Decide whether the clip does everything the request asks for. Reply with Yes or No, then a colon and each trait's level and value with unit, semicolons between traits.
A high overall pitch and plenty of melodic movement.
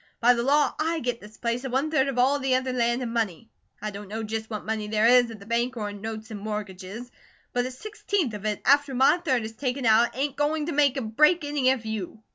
No: high, 240 Hz; average, 3.7 semitones